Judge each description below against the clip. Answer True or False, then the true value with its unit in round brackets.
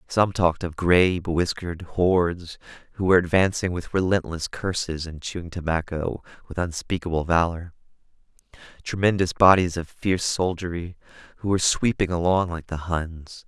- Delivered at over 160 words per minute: False (135 wpm)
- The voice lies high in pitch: False (85 Hz)